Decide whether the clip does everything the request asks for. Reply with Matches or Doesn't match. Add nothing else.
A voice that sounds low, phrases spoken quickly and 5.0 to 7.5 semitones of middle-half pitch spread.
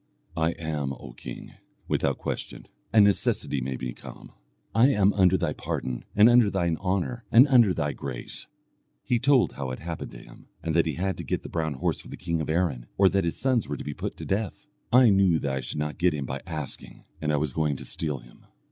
Matches